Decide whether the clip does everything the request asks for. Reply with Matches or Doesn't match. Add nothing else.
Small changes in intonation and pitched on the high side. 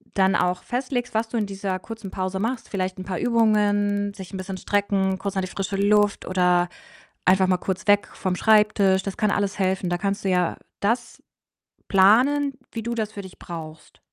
Matches